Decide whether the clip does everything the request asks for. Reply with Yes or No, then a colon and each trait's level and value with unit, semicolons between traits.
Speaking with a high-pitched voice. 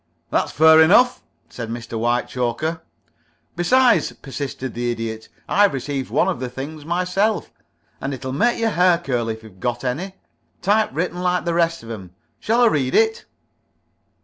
No: medium, 150 Hz